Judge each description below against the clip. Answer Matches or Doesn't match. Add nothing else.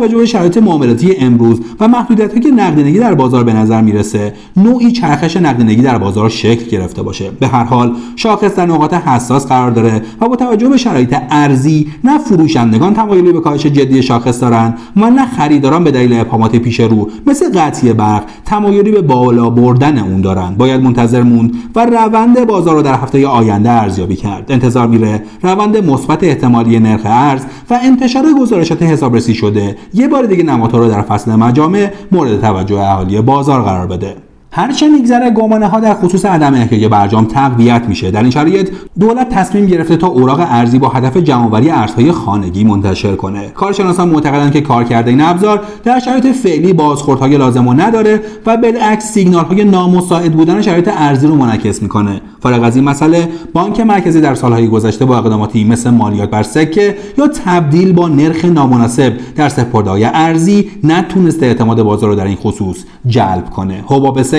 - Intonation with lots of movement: Matches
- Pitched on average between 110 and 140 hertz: Matches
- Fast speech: Matches